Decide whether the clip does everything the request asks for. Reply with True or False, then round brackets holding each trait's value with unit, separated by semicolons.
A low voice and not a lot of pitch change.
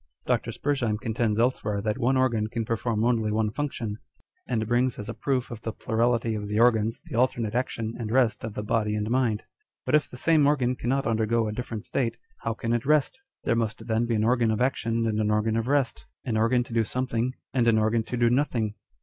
True (115 Hz; 2.3 semitones)